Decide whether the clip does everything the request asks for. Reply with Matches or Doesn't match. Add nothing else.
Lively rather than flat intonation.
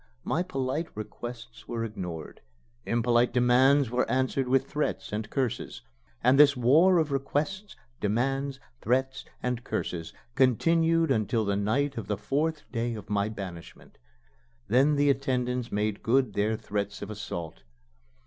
Doesn't match